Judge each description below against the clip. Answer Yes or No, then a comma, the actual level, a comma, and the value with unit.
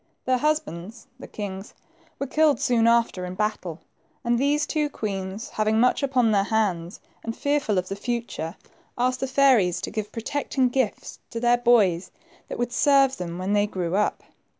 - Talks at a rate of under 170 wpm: No, average, 175 wpm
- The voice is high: Yes, high, 225 Hz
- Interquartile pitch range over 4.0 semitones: Yes, average, 4.8 semitones